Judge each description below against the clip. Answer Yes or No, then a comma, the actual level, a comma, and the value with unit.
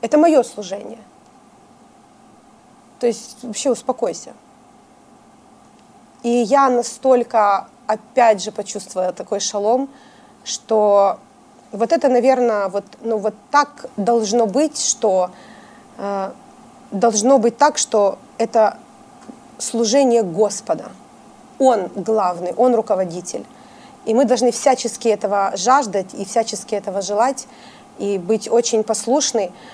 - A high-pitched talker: Yes, high, 235 Hz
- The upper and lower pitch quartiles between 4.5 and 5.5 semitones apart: No, average, 3.5 semitones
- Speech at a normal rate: No, slow, 105 wpm